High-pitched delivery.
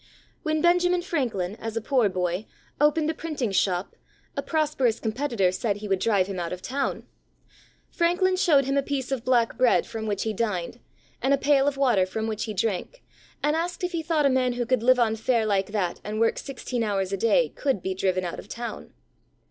Yes: high, 235 Hz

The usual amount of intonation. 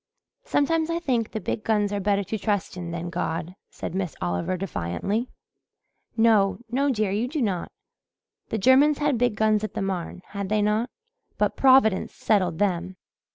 Yes: average, 4.2 semitones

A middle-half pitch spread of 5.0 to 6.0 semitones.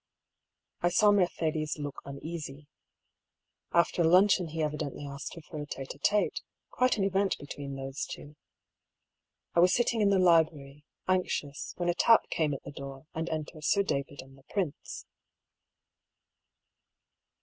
No: average, 4.2 semitones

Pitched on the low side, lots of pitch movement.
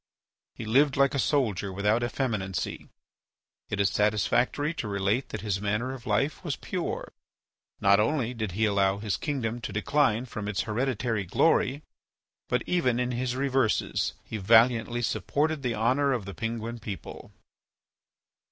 No: low, 115 Hz; average, 4.0 semitones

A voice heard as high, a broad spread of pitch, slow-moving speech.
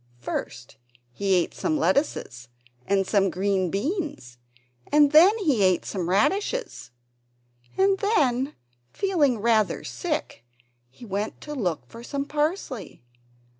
Yes: high, 235 Hz; wide, 8.4 semitones; slow, 120 wpm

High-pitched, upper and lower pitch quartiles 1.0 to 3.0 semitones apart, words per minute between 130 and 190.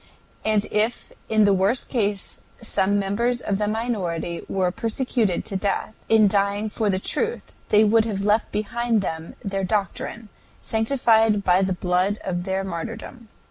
Yes: high, 205 Hz; narrow, 2.5 semitones; average, 155 wpm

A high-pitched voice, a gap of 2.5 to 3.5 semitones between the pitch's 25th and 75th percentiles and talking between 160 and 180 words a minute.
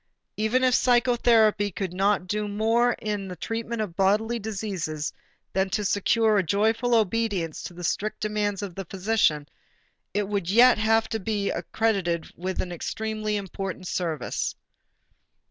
No: high, 210 Hz; average, 2.9 semitones; average, 145 wpm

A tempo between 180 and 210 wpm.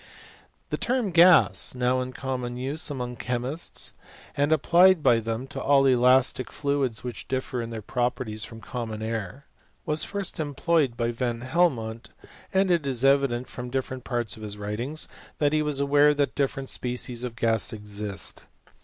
No: average, 160 wpm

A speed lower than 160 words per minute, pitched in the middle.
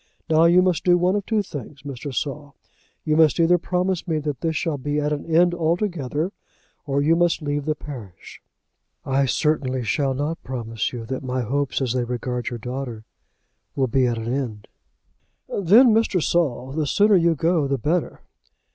No: average, 180 wpm; medium, 145 Hz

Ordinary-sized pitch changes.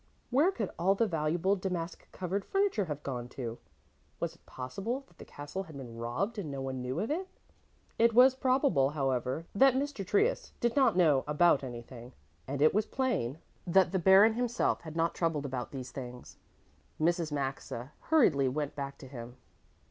No: wide, 8.3 semitones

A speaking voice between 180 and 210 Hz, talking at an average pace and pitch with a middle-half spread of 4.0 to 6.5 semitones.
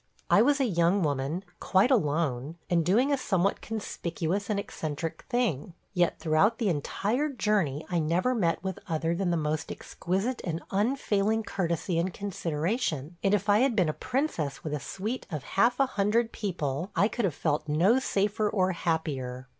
Yes: medium, 185 Hz; average, 175 wpm; average, 5.1 semitones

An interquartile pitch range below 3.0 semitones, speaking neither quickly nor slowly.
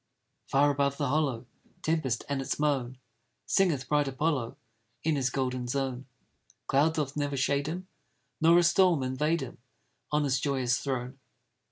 Yes: narrow, 2.6 semitones; average, 150 wpm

